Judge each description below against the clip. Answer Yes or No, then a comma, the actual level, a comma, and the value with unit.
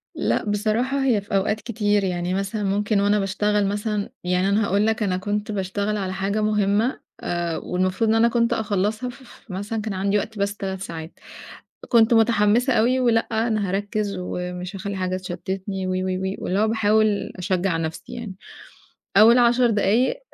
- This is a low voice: No, high, 205 Hz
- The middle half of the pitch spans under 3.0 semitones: Yes, narrow, 2.5 semitones